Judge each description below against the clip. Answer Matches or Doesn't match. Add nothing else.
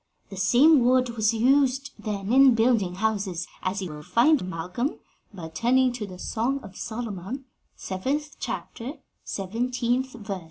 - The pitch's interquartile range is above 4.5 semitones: Matches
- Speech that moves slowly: Doesn't match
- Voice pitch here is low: Doesn't match